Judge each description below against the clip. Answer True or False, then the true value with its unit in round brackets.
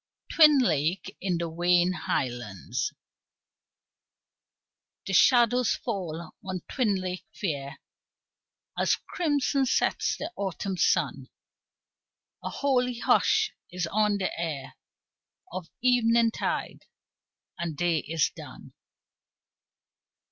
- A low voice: False (185 Hz)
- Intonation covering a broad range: True (6.5 semitones)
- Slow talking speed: True (95 wpm)